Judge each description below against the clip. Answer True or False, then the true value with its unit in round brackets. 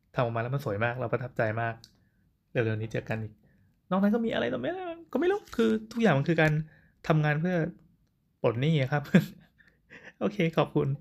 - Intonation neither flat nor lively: False (7.8 semitones)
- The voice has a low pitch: False (150 Hz)